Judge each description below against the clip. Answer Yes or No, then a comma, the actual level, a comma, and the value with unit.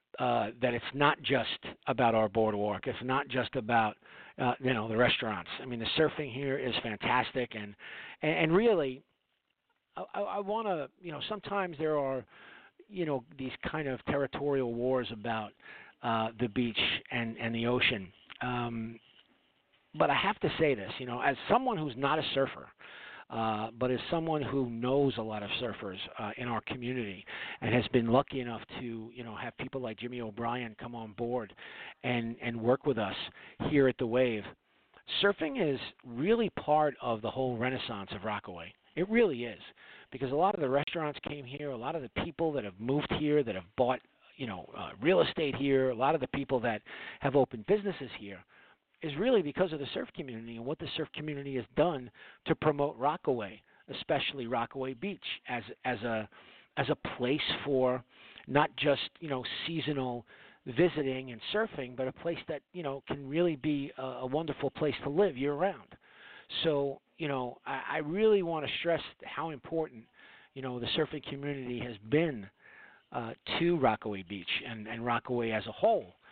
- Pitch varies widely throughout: No, average, 4.0 semitones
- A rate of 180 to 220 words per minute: Yes, average, 185 wpm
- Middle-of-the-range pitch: No, low, 130 Hz